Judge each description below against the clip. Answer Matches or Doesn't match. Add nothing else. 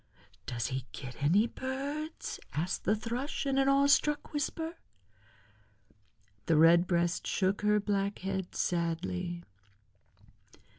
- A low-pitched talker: Doesn't match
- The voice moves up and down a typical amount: Doesn't match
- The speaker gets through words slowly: Matches